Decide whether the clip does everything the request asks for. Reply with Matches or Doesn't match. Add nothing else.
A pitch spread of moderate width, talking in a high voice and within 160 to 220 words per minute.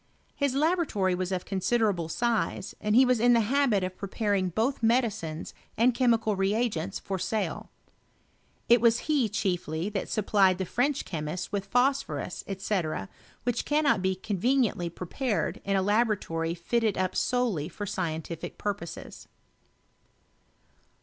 Doesn't match